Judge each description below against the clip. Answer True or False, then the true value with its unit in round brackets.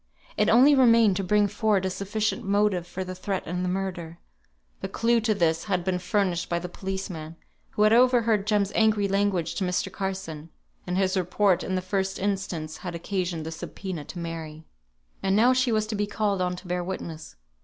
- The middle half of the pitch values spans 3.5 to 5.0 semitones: False (2.7 semitones)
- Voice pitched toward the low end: False (190 Hz)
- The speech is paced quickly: False (195 wpm)